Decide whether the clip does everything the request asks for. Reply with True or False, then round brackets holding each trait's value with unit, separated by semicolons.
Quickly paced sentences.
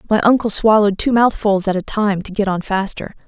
True (220 wpm)